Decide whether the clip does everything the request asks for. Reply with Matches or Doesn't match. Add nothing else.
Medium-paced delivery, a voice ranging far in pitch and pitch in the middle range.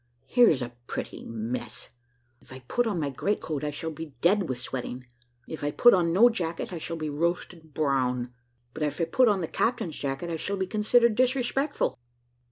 Matches